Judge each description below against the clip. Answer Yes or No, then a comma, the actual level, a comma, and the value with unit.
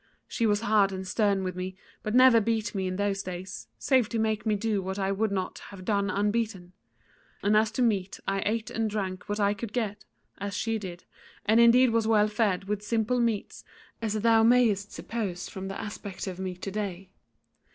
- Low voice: No, high, 205 Hz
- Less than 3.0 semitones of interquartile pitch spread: Yes, narrow, 2.5 semitones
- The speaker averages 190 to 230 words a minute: Yes, fast, 205 wpm